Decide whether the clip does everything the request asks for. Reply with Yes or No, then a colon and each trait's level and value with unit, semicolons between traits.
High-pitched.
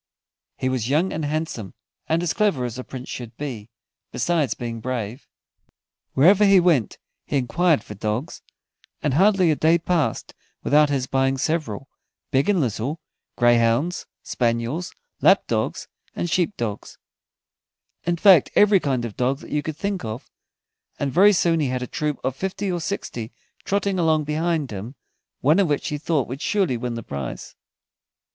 No: medium, 145 Hz